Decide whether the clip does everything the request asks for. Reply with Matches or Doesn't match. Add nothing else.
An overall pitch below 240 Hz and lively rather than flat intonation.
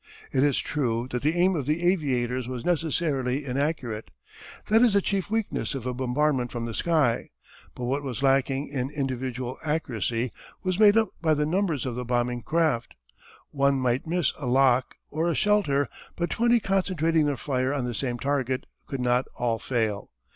Doesn't match